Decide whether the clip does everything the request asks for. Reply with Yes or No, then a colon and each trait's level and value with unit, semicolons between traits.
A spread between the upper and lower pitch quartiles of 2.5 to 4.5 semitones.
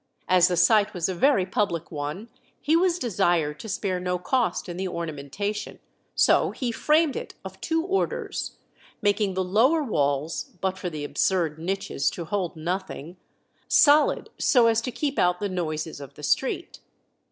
No: average, 5.0 semitones